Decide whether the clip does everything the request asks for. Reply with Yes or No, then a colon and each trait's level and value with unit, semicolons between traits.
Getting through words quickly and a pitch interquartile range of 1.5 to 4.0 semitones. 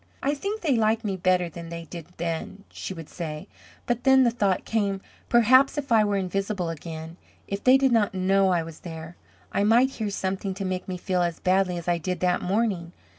No: fast, 215 wpm; average, 4.5 semitones